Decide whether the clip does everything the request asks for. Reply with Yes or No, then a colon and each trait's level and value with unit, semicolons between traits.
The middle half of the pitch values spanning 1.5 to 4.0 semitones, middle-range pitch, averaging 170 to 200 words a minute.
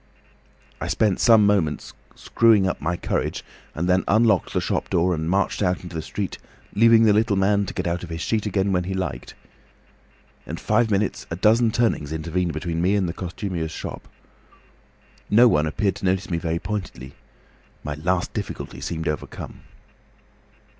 No: average, 3.6 semitones; very low, 95 Hz; average, 175 wpm